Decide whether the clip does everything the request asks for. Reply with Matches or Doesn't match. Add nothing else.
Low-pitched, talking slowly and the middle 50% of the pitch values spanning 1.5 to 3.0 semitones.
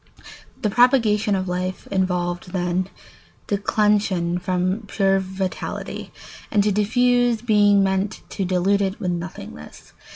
Doesn't match